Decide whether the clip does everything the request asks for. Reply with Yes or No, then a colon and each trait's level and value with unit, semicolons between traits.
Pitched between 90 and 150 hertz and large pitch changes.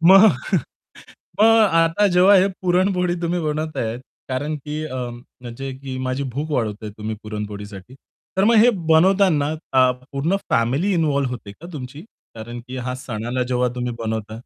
Yes: medium, 140 Hz; wide, 6.6 semitones